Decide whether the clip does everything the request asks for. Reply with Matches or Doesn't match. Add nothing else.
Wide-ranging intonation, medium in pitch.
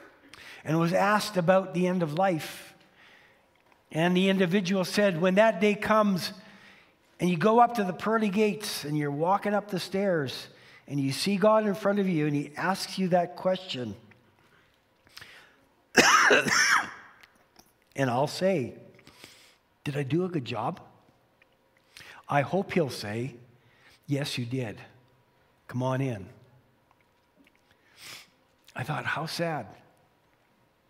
Matches